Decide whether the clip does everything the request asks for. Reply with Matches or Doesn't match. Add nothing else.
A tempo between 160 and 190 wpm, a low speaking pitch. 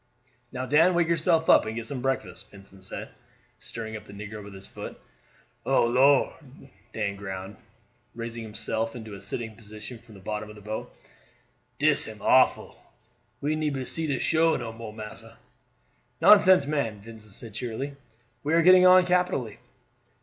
Matches